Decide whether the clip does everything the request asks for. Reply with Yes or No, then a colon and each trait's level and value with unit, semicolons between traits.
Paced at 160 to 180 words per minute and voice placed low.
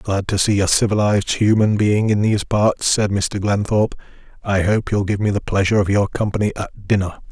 No: fast, 205 wpm; low, 100 Hz